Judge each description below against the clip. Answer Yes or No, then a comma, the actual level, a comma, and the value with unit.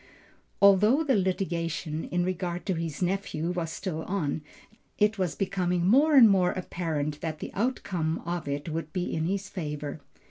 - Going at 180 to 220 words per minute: No, average, 165 wpm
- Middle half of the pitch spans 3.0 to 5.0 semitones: Yes, average, 3.5 semitones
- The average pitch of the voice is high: No, medium, 180 Hz